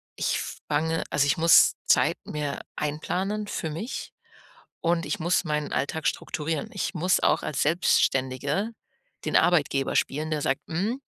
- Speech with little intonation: No, average, 3.3 semitones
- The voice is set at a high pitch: No, medium, 160 Hz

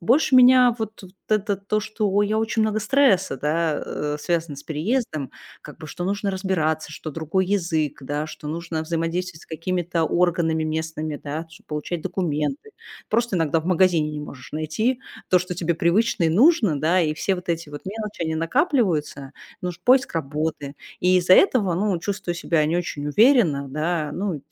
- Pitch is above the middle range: No, medium, 170 Hz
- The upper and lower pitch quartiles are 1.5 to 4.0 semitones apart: No, average, 4.6 semitones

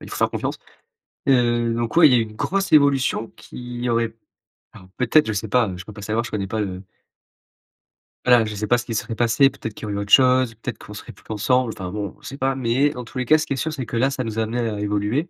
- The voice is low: Yes, low, 120 Hz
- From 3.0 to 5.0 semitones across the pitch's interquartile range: Yes, average, 3.3 semitones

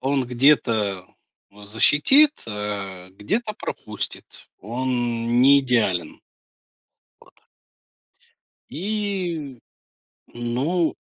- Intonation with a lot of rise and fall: Yes, wide, 7.6 semitones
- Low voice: Yes, low, 130 Hz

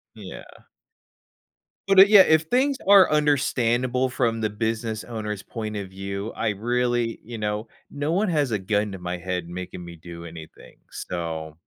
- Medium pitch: No, low, 110 Hz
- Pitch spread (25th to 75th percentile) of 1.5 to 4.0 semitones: No, wide, 5.5 semitones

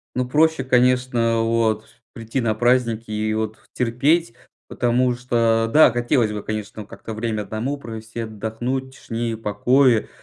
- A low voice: Yes, low, 115 Hz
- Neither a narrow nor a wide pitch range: No, narrow, 2.3 semitones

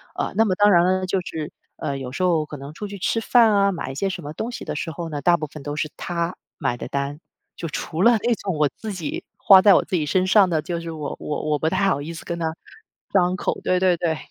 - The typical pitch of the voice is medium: Yes, medium, 170 Hz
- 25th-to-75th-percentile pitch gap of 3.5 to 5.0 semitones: Yes, average, 3.8 semitones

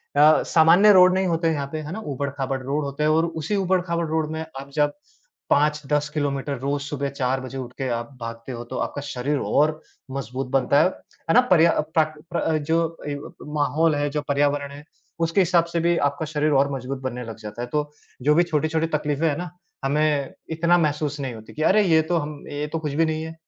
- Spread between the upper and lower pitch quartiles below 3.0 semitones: Yes, narrow, 2.6 semitones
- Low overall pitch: No, medium, 150 Hz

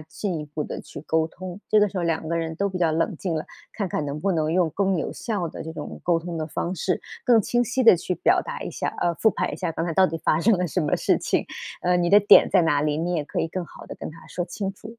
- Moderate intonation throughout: Yes, average, 3.0 semitones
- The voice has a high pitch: No, medium, 175 Hz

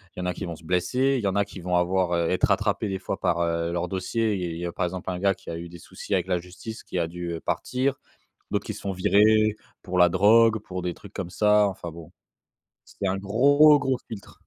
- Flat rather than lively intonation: No, average, 3.2 semitones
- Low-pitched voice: Yes, very low, 95 Hz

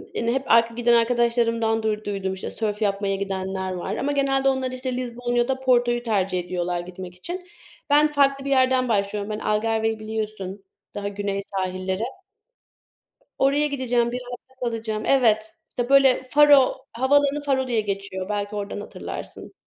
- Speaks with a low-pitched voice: No, high, 230 Hz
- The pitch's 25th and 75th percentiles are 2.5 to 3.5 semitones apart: No, average, 4.5 semitones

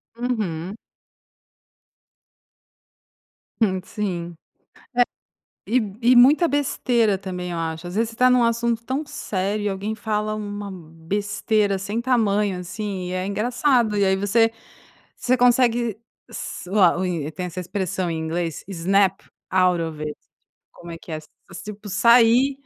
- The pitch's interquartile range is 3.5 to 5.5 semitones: Yes, average, 4.3 semitones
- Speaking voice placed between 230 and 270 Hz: No, high, 205 Hz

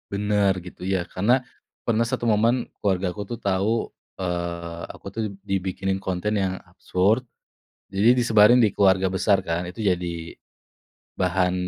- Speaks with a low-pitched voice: Yes, very low, 95 Hz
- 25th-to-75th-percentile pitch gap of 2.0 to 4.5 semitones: Yes, narrow, 2.5 semitones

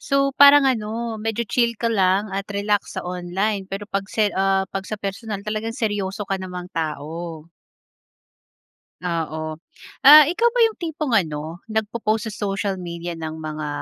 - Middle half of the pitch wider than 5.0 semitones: No, average, 3.9 semitones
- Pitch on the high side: Yes, high, 200 Hz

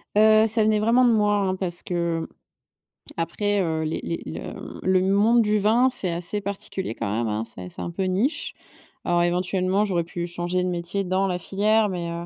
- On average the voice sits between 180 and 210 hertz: Yes, medium, 185 Hz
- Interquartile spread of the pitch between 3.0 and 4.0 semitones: Yes, average, 3.4 semitones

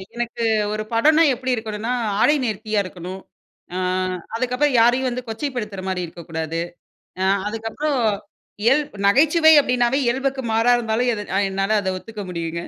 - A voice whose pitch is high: Yes, high, 230 Hz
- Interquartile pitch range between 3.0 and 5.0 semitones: Yes, average, 4.2 semitones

